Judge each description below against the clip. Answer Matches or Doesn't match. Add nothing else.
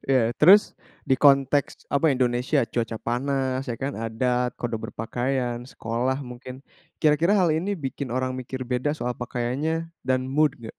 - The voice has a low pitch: Matches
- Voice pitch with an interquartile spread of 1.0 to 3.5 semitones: Matches